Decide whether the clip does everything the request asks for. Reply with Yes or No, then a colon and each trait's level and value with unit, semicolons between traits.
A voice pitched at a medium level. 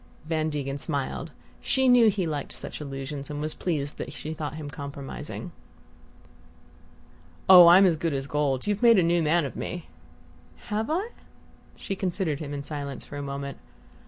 Yes: medium, 155 Hz